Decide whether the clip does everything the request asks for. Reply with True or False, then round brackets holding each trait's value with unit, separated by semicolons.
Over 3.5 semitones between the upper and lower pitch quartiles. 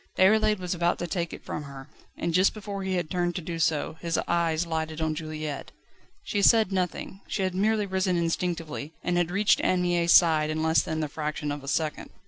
False (2.9 semitones)